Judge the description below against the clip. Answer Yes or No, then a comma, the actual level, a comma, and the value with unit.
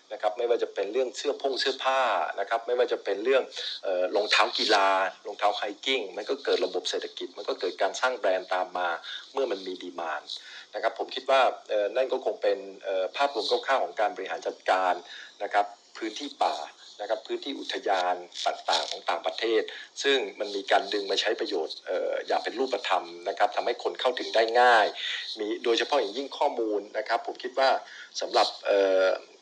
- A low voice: No, very high, 360 Hz